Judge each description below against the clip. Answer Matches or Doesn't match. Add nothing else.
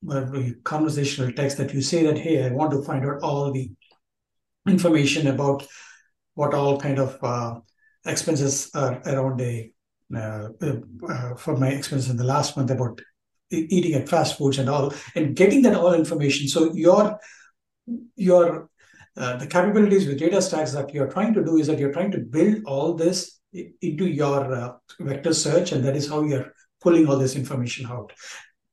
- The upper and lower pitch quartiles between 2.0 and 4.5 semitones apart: Matches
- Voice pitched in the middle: Matches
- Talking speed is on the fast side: Doesn't match